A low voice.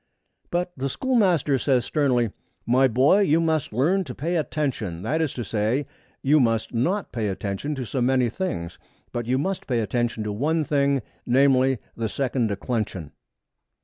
Yes: low, 130 Hz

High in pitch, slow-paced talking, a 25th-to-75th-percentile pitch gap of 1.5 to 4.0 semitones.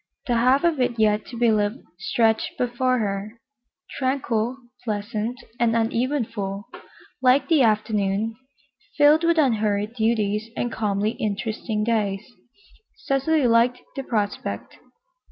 Yes: high, 230 Hz; slow, 120 wpm; average, 3.1 semitones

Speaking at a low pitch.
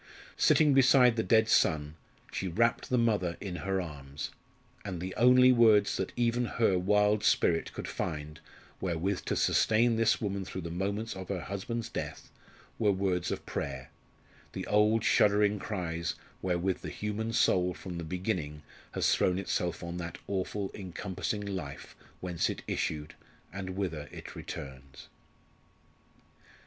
Yes: very low, 95 Hz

